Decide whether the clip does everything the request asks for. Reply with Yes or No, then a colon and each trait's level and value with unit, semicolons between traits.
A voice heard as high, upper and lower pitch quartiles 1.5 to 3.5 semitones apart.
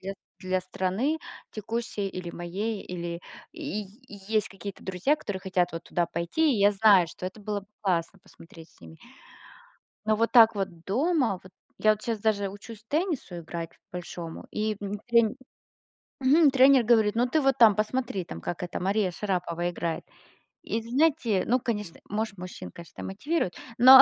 No: high, 205 Hz; average, 4.3 semitones